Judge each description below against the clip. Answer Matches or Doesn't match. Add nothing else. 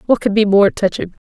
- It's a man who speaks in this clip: Doesn't match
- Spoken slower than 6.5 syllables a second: Matches